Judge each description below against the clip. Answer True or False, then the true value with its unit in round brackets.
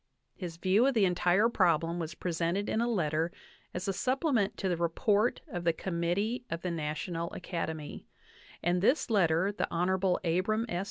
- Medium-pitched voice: True (180 Hz)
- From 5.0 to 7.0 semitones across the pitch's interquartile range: False (3.6 semitones)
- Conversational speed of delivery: True (170 wpm)